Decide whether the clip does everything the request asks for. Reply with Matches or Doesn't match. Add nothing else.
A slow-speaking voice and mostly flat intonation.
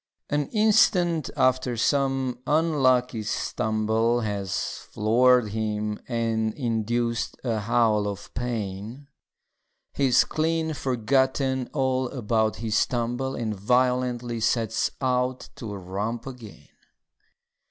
Doesn't match